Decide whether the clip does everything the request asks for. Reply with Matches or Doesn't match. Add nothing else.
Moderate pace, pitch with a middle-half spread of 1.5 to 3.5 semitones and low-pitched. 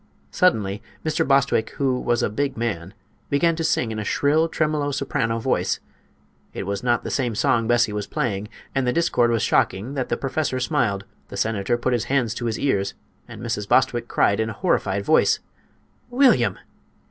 Doesn't match